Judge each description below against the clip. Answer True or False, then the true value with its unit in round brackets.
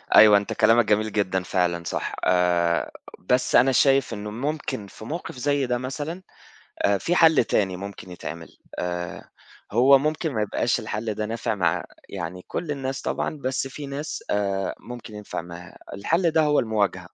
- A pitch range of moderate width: False (6.5 semitones)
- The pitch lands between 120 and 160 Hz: False (110 Hz)